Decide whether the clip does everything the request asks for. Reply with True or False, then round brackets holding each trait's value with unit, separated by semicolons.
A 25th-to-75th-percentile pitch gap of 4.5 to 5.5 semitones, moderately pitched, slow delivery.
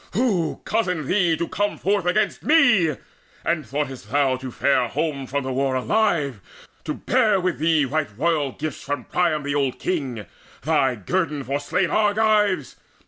False (5.2 semitones; 155 Hz; 160 wpm)